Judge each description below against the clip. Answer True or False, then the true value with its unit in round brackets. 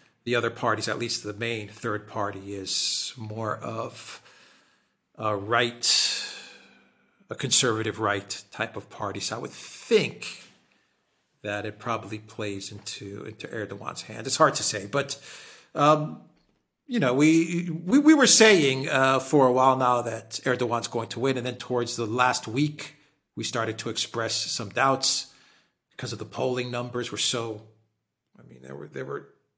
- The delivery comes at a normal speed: True (160 wpm)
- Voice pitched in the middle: False (115 Hz)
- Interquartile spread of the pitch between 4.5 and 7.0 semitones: False (3.7 semitones)